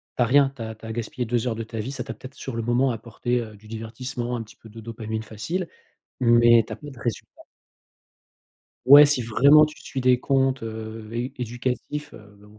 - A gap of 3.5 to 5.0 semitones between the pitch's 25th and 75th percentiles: No, average, 2.7 semitones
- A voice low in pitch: Yes, low, 120 Hz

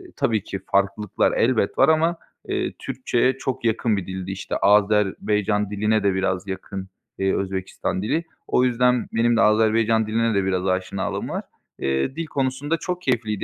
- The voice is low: Yes, low, 105 Hz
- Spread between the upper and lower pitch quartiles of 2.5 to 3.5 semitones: No, average, 3.9 semitones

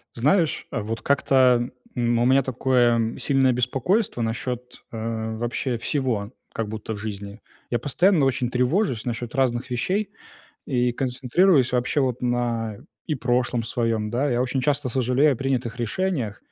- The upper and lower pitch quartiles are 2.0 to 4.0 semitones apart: Yes, narrow, 2.5 semitones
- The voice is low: Yes, low, 125 Hz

